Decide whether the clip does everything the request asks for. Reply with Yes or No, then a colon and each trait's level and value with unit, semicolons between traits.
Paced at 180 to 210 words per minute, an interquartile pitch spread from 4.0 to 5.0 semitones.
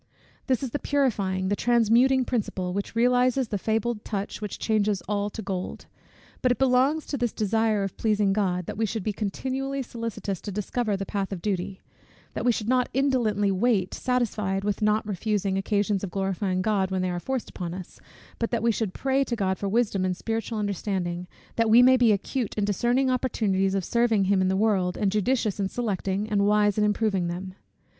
No: average, 200 wpm; average, 3.5 semitones